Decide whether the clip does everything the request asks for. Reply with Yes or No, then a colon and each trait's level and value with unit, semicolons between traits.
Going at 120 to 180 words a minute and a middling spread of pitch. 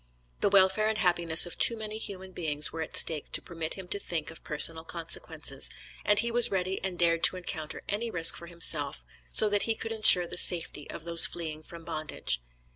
No: fast, 205 wpm; average, 3.6 semitones